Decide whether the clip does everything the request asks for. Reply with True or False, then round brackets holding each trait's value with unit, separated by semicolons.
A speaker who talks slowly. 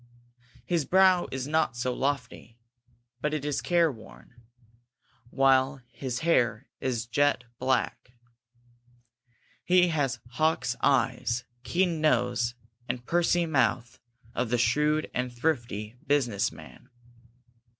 True (115 wpm)